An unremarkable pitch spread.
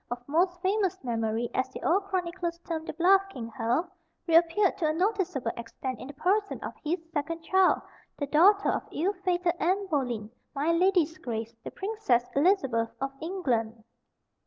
No: wide, 6.7 semitones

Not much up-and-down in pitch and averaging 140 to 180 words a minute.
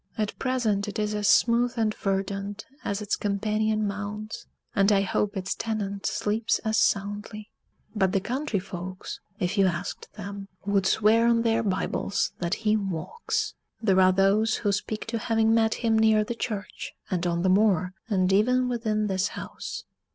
Yes: narrow, 2.1 semitones; average, 170 wpm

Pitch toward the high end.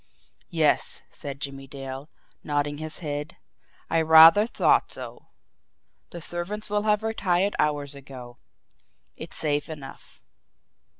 No: medium, 150 Hz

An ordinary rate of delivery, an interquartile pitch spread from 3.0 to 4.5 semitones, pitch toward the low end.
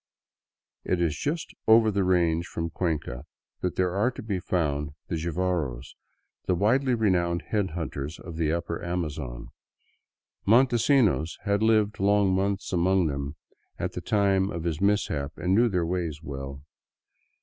Yes: average, 150 wpm; average, 4.1 semitones; very low, 90 Hz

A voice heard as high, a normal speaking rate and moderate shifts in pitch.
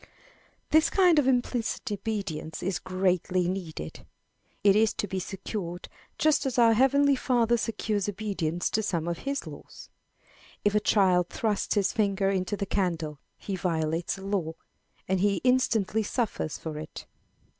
Yes: high, 200 Hz; average, 150 wpm; average, 4.0 semitones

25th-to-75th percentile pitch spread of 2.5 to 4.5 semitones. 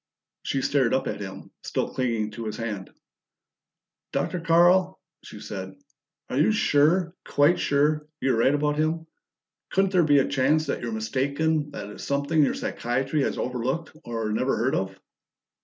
No: average, 5.2 semitones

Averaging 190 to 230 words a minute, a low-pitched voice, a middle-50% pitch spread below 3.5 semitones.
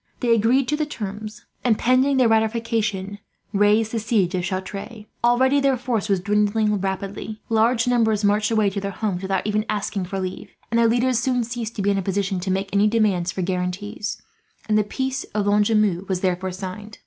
No: average, 195 wpm; high, 210 Hz; average, 2.8 semitones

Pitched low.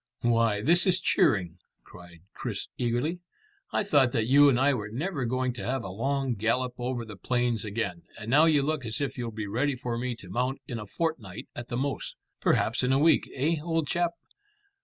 Yes: low, 125 Hz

